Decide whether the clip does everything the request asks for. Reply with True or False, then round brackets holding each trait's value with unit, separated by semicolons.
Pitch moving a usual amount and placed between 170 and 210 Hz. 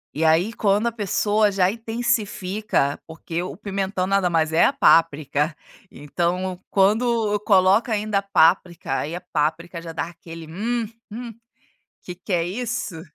True (4.2 semitones; 185 Hz)